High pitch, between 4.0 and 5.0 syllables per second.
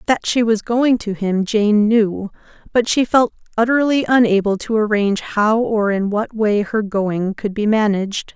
Yes: high, 215 Hz; 4.4 syllables/s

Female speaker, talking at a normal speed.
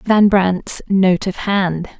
Yes: female; average, 150 wpm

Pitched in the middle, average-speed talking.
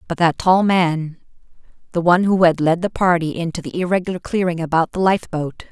Yes: medium, 175 Hz; average, 190 wpm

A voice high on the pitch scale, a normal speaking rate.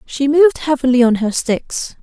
Yes: very high, 270 Hz; average, 180 wpm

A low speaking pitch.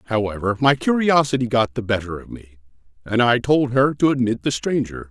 Yes: low, 120 Hz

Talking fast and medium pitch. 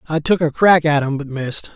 Yes: fast, 275 wpm; medium, 155 Hz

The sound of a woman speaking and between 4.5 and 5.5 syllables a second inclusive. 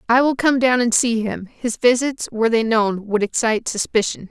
Yes: female; 5.2 syllables/s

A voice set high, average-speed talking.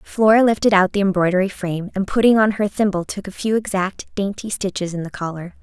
No: high, 195 Hz; fast, 215 wpm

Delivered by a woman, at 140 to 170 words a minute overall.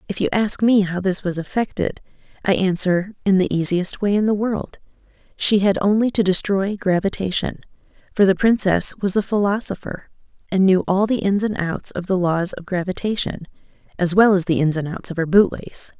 No: female; average, 195 wpm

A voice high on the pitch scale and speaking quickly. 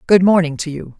No: medium, 170 Hz; fast, 240 wpm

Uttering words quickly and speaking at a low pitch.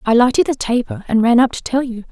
No: fast, 285 wpm; high, 245 Hz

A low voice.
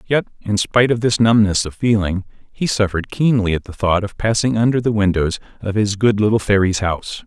Yes: low, 105 Hz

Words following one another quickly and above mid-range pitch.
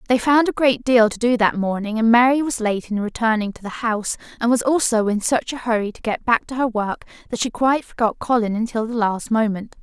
Yes: fast, 245 wpm; high, 230 Hz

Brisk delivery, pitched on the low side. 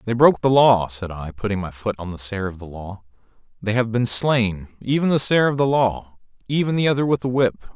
Yes: fast, 230 wpm; low, 110 Hz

